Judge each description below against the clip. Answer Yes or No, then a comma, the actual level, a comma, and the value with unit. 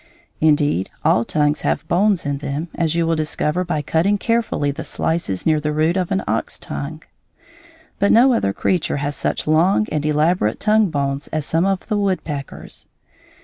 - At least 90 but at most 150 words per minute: No, average, 175 wpm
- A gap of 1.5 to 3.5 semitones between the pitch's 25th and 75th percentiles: No, average, 4.0 semitones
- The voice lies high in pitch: No, medium, 160 Hz